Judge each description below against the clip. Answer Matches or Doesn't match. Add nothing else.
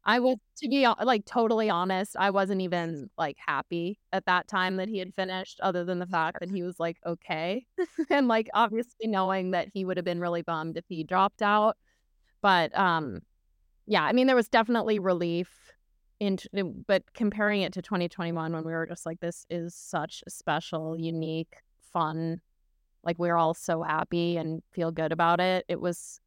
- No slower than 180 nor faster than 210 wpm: Matches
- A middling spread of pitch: Matches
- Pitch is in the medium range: Matches